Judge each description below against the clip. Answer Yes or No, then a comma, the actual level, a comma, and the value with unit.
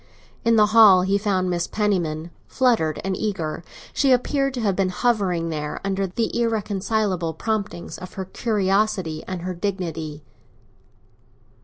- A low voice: No, high, 195 Hz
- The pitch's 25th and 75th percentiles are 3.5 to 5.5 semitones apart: Yes, average, 3.8 semitones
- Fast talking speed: No, average, 140 wpm